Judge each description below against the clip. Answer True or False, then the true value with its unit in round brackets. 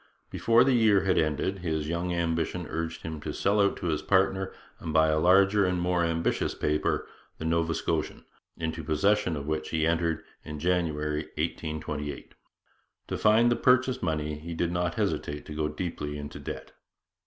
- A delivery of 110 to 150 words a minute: False (175 wpm)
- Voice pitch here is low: True (85 Hz)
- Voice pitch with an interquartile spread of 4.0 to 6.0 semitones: False (3.0 semitones)